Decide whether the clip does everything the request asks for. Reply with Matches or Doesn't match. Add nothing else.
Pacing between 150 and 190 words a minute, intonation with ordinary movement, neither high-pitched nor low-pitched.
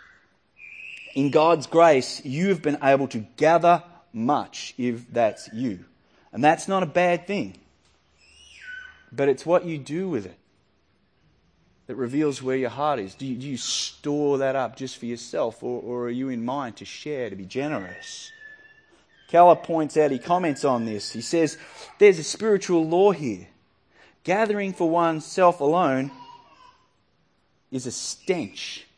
Doesn't match